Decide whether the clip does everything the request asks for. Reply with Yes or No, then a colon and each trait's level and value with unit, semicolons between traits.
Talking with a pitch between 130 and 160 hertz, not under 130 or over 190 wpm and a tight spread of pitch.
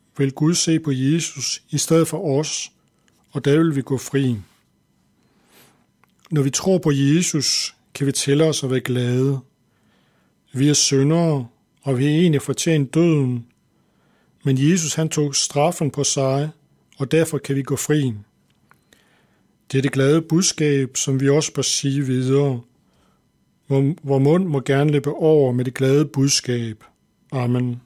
Yes: medium, 140 Hz; average, 155 wpm; narrow, 2.3 semitones